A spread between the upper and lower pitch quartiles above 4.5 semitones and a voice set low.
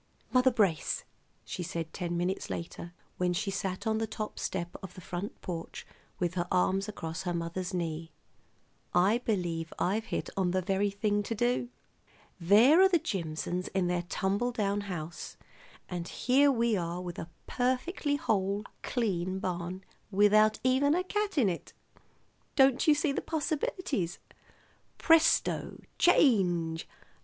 No: wide, 5.5 semitones; high, 195 Hz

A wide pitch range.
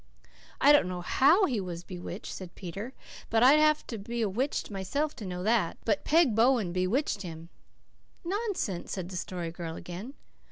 Yes: wide, 6.9 semitones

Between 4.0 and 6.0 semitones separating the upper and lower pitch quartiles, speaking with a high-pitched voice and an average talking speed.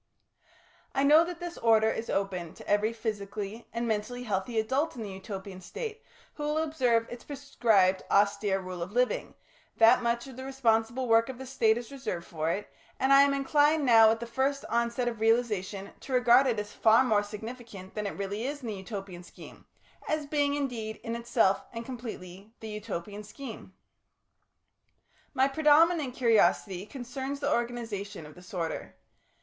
Yes: average, 4.3 semitones; high, 230 Hz; average, 175 wpm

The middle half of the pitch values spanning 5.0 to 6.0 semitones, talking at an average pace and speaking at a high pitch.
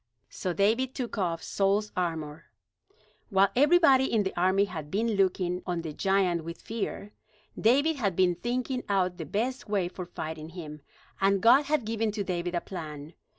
No: average, 4.6 semitones; average, 170 wpm; high, 195 Hz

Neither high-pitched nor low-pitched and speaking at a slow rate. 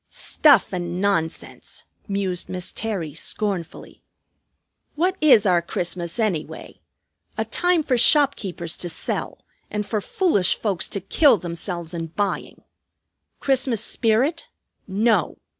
No: high, 200 Hz; slow, 115 wpm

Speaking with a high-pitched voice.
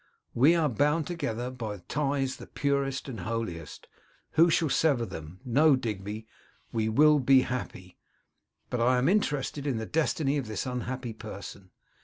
No: low, 130 Hz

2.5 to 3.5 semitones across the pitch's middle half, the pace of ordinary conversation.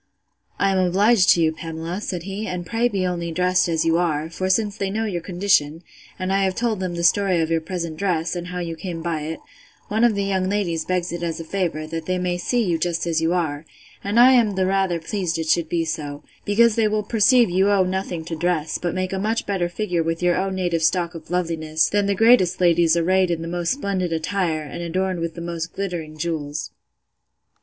No: average, 2.9 semitones; fast, 230 wpm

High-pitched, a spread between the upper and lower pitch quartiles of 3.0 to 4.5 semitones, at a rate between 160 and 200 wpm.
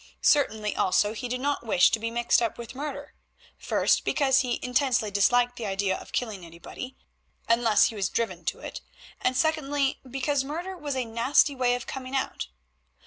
Yes: high, 245 Hz; average, 3.5 semitones; average, 180 wpm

